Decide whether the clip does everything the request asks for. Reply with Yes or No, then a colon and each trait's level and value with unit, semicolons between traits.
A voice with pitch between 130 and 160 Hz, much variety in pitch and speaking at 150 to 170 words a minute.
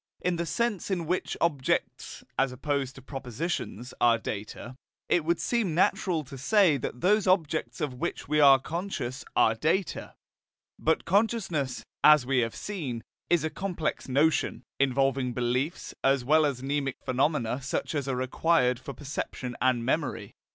No: medium, 140 Hz; average, 4.7 semitones; average, 155 wpm